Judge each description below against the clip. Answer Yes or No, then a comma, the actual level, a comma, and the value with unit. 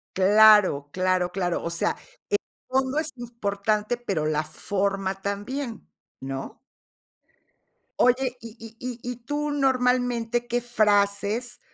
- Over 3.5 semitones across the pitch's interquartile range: Yes, average, 4.1 semitones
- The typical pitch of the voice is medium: No, high, 220 Hz